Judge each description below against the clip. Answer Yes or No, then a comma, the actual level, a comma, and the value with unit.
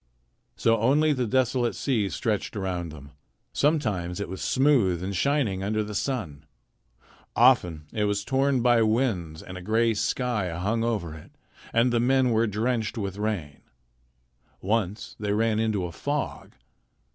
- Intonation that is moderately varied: Yes, average, 4.6 semitones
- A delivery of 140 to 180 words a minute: Yes, average, 150 wpm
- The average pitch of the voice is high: No, low, 110 Hz